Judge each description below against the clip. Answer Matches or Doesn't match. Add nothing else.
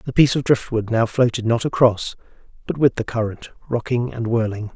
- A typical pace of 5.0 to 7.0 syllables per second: Matches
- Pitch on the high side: Doesn't match